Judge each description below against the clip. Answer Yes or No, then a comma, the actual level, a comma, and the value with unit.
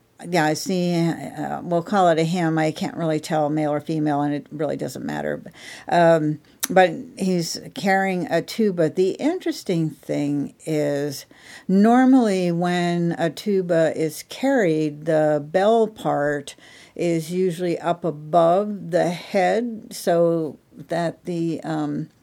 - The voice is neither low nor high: Yes, medium, 170 Hz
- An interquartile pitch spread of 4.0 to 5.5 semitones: No, average, 3.3 semitones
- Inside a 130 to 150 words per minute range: Yes, slow, 135 wpm